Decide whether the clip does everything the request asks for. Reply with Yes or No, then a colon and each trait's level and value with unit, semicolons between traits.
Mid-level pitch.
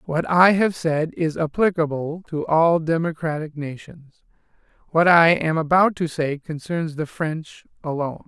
Yes: medium, 160 Hz